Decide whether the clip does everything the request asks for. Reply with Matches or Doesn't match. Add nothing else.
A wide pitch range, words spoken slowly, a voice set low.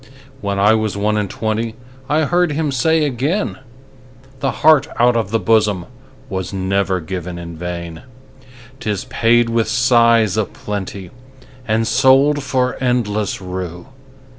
Doesn't match